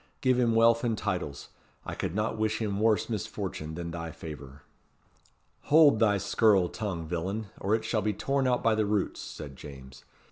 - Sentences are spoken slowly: No, average, 180 wpm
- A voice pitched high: No, low, 105 Hz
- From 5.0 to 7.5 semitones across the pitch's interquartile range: Yes, average, 5.3 semitones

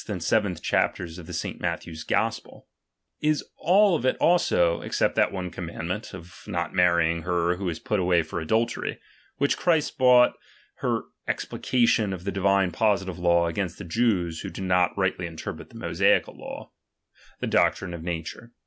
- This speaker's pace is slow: No, average, 165 wpm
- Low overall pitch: Yes, very low, 90 Hz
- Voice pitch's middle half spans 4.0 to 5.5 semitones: Yes, average, 4.5 semitones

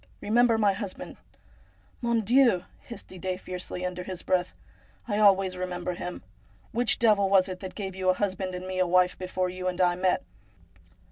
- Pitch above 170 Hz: Yes, medium, 185 Hz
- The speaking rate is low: No, average, 200 wpm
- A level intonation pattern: Yes, narrow, 2.0 semitones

